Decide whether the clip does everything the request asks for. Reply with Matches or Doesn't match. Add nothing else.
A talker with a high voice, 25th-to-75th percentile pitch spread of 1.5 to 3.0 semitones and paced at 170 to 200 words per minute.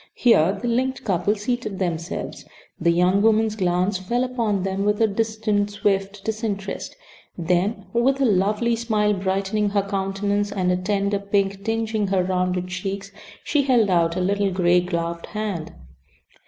Doesn't match